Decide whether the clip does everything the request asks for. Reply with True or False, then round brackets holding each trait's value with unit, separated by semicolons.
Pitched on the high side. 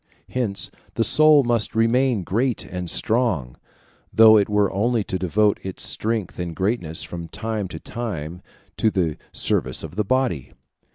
False (105 Hz)